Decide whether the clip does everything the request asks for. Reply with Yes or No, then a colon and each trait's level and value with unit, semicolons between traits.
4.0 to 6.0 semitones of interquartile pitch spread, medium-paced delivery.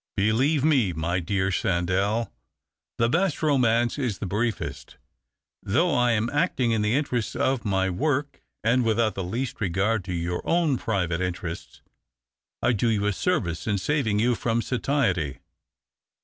Yes: average, 5.2 semitones; average, 150 wpm